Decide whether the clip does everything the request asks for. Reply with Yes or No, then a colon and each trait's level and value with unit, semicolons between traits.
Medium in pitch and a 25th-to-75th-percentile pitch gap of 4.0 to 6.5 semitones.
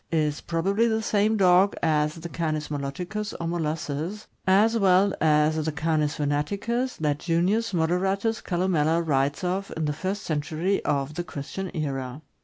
Yes: medium, 165 Hz; average, 4.4 semitones